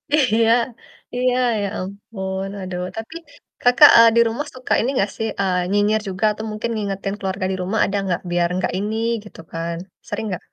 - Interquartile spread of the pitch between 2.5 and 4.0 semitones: Yes, average, 3.0 semitones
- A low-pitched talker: No, high, 205 Hz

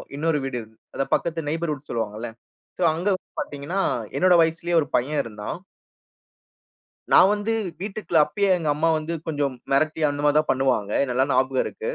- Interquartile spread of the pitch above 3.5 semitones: Yes, average, 3.9 semitones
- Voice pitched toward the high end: No, medium, 150 Hz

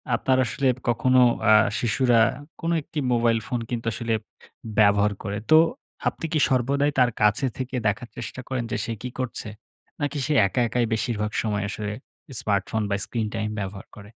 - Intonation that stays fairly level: No, average, 3.4 semitones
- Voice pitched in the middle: No, low, 120 Hz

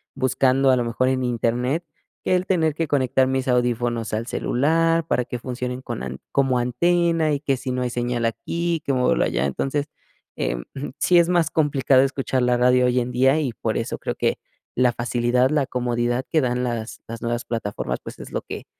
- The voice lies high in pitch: No, low, 125 Hz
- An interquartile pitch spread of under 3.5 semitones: Yes, average, 2.9 semitones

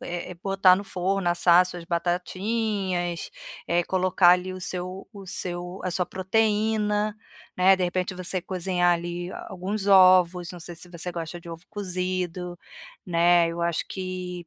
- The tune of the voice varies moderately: No, narrow, 1.4 semitones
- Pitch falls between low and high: Yes, medium, 180 Hz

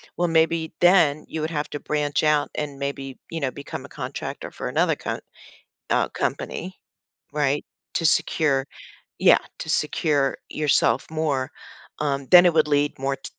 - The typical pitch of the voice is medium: Yes, medium, 150 Hz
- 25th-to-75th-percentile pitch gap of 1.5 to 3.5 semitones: Yes, narrow, 2.4 semitones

